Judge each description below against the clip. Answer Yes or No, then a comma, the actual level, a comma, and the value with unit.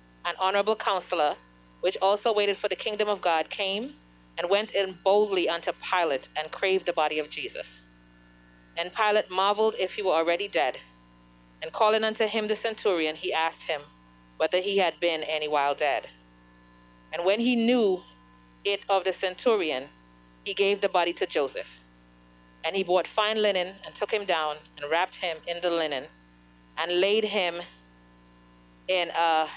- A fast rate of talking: No, average, 165 wpm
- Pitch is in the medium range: Yes, medium, 170 Hz